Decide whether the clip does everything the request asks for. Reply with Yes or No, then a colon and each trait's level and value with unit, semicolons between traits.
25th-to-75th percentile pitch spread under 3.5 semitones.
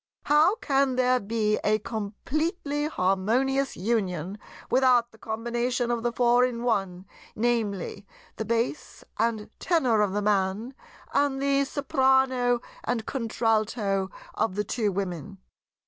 No: average, 4.0 semitones